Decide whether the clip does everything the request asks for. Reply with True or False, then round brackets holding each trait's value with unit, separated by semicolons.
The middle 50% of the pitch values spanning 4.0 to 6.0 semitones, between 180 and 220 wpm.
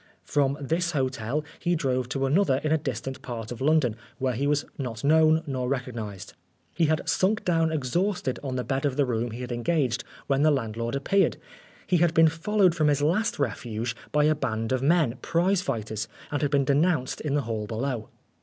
True (4.4 semitones; 200 wpm)